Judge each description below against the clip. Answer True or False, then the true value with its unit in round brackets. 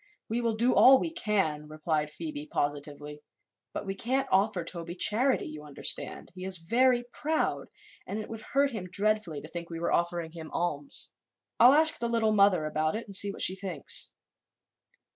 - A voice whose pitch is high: True (195 Hz)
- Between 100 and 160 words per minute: False (180 wpm)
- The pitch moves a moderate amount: False (6.4 semitones)